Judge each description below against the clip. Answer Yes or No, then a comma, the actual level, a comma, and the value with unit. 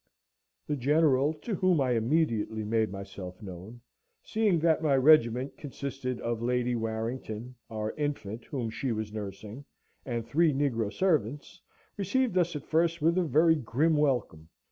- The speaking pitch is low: Yes, low, 130 Hz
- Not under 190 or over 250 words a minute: No, average, 145 wpm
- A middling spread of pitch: No, wide, 5.9 semitones